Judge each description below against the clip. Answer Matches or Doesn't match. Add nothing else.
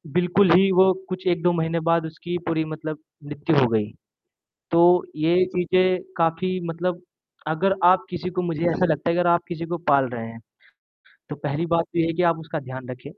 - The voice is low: Doesn't match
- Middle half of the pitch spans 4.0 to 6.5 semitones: Doesn't match